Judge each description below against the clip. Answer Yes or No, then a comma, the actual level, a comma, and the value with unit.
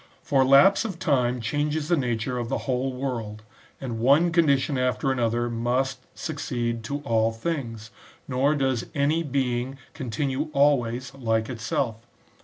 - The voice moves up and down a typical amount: Yes, average, 3.2 semitones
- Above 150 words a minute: No, average, 145 wpm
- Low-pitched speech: Yes, low, 130 Hz